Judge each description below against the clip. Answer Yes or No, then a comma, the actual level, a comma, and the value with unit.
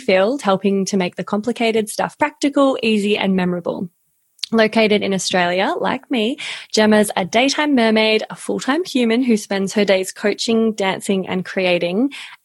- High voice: Yes, high, 215 Hz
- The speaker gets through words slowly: No, average, 155 wpm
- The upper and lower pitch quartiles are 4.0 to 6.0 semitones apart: No, average, 3.1 semitones